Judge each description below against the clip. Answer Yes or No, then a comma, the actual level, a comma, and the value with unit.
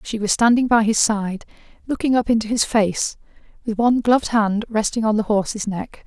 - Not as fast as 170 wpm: No, average, 200 wpm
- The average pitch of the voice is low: No, high, 220 Hz